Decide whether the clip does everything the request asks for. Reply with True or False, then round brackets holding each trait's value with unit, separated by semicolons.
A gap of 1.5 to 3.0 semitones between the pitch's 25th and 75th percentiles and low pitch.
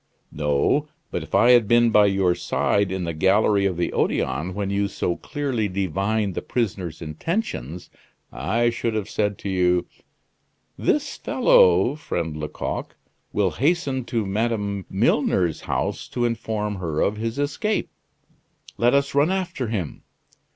False (4.6 semitones; 105 Hz)